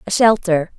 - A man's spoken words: No, female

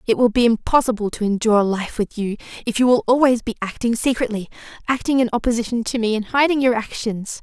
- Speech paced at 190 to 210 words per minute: Yes, average, 195 wpm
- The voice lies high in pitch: Yes, high, 230 Hz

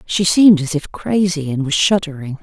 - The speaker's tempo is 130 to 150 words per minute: No, average, 200 wpm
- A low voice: No, medium, 165 Hz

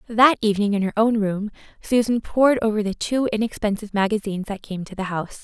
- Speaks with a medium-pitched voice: No, high, 210 Hz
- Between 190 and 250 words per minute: Yes, average, 200 wpm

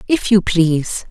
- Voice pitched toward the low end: No, high, 190 Hz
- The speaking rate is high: No, average, 165 wpm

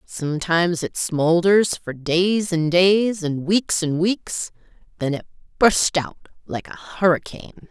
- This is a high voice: No, medium, 175 Hz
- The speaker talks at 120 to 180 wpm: Yes, average, 140 wpm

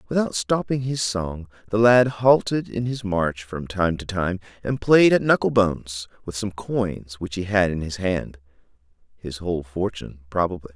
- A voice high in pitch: No, low, 100 Hz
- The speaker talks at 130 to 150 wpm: No, average, 175 wpm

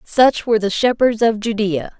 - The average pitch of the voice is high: Yes, high, 225 Hz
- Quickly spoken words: No, average, 180 wpm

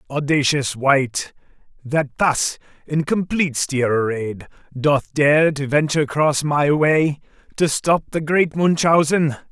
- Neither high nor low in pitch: Yes, medium, 145 Hz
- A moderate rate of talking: No, slow, 125 wpm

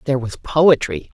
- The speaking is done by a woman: Yes, female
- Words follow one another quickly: No, average, 150 wpm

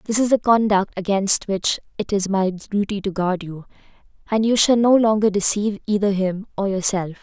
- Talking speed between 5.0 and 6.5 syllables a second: Yes, 5.2 syllables/s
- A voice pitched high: Yes, high, 200 Hz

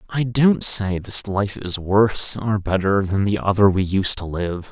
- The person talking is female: No, male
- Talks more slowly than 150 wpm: No, fast, 205 wpm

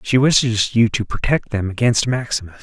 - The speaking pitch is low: Yes, low, 115 Hz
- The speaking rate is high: No, average, 185 wpm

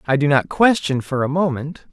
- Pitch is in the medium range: Yes, medium, 150 Hz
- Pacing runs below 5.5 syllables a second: Yes, 5.1 syllables/s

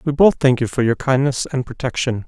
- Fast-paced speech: Yes, fast, 235 wpm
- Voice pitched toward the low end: Yes, low, 130 Hz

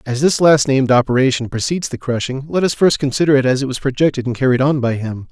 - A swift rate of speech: Yes, fast, 250 wpm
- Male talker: Yes, male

